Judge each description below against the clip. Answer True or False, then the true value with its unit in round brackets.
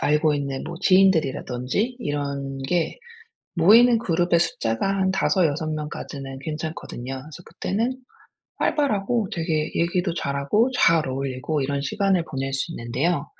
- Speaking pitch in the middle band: True (160 Hz)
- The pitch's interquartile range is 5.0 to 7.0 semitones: True (5.4 semitones)